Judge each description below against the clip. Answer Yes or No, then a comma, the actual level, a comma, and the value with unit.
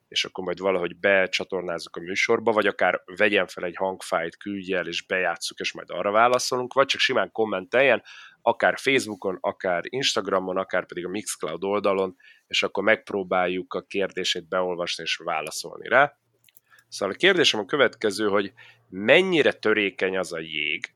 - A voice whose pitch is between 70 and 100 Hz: Yes, very low, 95 Hz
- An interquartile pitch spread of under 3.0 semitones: Yes, narrow, 2.4 semitones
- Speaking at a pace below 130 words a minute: No, fast, 155 wpm